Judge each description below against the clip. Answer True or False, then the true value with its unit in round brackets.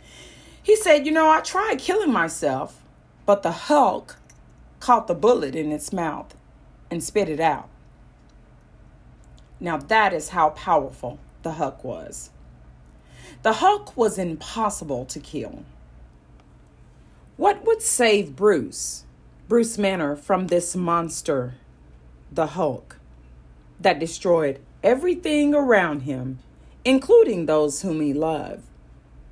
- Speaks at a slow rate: True (115 wpm)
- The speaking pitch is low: False (165 Hz)